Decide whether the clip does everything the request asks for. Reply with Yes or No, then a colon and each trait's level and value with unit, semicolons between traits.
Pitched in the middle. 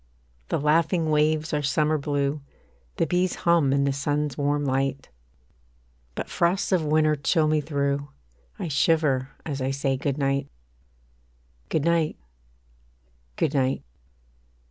Yes: medium, 145 Hz